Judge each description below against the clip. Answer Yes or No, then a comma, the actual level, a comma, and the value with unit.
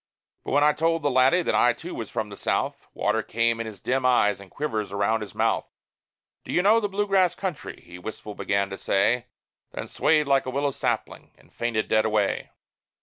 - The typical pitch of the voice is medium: No, low, 125 Hz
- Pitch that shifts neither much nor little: No, wide, 6.0 semitones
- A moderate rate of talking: No, fast, 210 wpm